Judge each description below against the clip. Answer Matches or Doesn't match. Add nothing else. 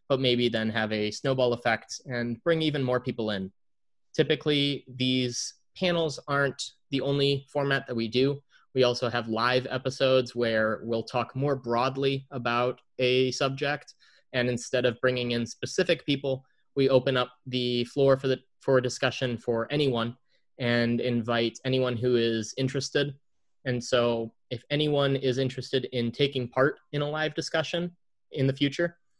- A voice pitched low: Matches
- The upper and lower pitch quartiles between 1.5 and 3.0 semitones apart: Matches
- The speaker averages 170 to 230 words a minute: Doesn't match